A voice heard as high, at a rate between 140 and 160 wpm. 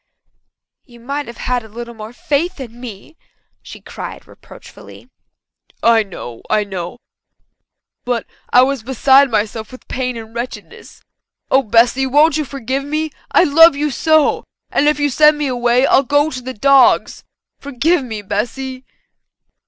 Yes: very high, 255 Hz; average, 150 wpm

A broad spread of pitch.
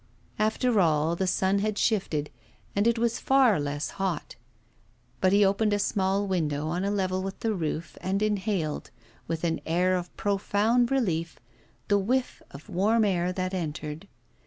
No: average, 3.7 semitones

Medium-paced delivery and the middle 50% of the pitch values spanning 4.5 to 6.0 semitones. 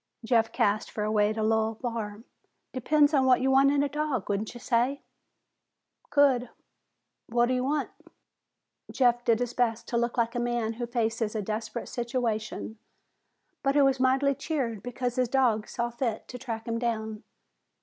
No: average, 175 wpm; narrow, 2.6 semitones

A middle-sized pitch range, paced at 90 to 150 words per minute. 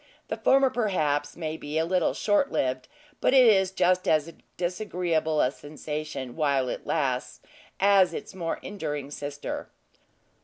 Yes: average, 4.4 semitones; average, 145 wpm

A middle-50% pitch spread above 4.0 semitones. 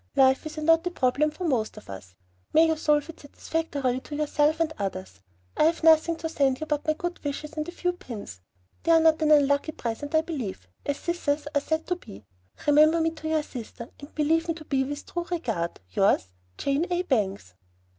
No: average, 3.6 semitones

